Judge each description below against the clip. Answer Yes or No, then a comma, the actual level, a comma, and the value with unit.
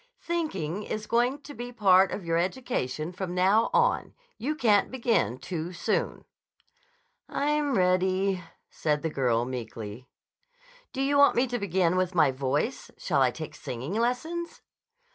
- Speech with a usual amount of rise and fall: No, wide, 7.6 semitones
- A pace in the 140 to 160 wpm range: Yes, average, 145 wpm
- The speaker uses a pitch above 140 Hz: Yes, high, 190 Hz